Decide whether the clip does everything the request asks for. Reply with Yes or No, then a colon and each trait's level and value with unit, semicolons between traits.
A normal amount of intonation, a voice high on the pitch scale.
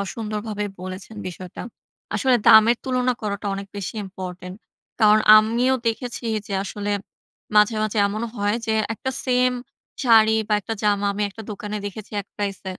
No: narrow, 2.0 semitones; high, 210 Hz